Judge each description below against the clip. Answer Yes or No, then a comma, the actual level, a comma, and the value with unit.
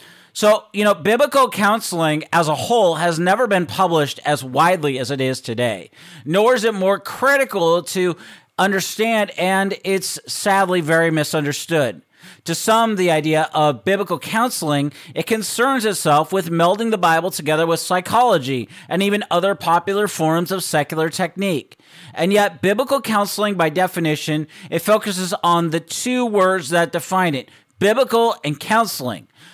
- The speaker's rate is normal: Yes, average, 150 wpm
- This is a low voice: No, medium, 180 Hz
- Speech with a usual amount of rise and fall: Yes, average, 4.3 semitones